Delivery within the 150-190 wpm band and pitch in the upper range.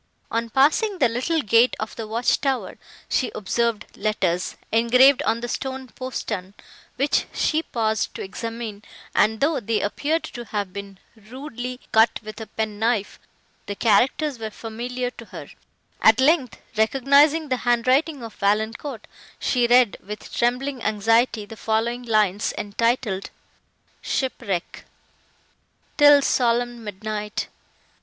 No: slow, 135 wpm; high, 235 Hz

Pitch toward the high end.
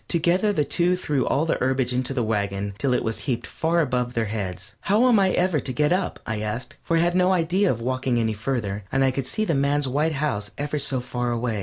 No: low, 130 Hz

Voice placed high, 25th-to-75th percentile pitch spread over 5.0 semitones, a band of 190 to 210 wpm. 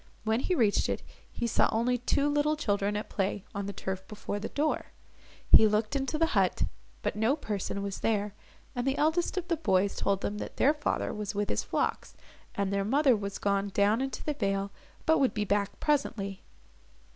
Yes: high, 215 Hz; wide, 5.6 semitones; average, 200 wpm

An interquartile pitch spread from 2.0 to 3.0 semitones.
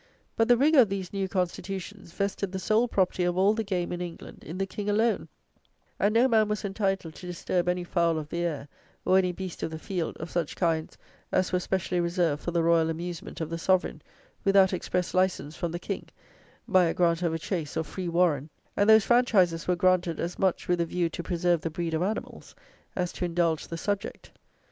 Yes: narrow, 2.4 semitones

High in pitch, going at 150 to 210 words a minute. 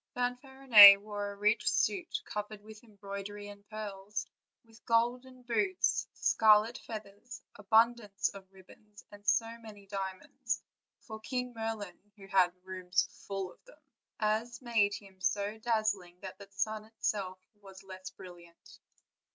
No: high, 210 Hz; slow, 135 wpm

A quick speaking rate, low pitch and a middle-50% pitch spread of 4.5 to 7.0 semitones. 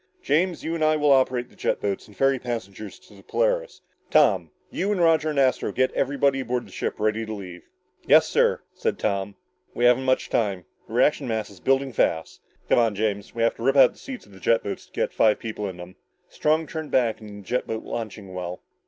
Yes: fast, 230 wpm; low, 115 Hz; average, 5.0 semitones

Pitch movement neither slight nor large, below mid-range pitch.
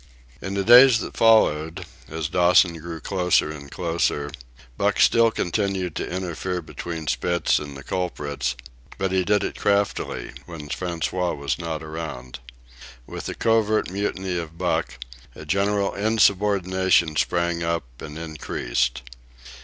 Yes: average, 3.9 semitones; very low, 85 Hz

